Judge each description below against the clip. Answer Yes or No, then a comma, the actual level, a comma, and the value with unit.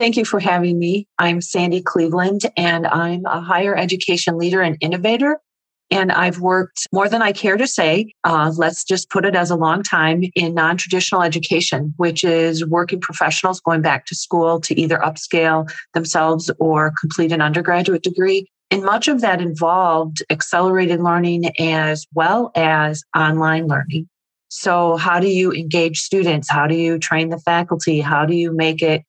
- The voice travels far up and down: No, narrow, 2.4 semitones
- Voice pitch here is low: No, medium, 170 Hz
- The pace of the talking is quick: No, average, 175 wpm